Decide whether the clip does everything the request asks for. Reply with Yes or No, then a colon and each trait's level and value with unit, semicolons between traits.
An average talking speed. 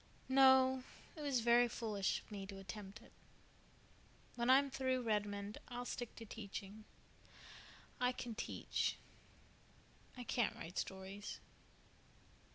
No: slow, 120 wpm